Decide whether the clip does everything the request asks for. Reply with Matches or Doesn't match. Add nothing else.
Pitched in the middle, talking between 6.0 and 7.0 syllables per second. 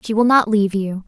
Doesn't match